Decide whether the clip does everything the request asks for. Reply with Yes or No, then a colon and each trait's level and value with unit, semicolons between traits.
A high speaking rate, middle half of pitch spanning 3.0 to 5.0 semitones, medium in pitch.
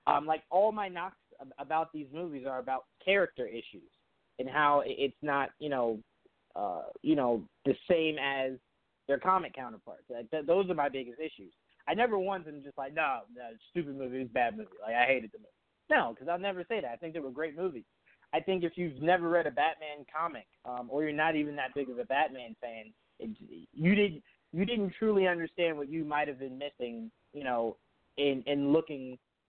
Yes: fast, 215 wpm; average, 4.7 semitones; medium, 145 Hz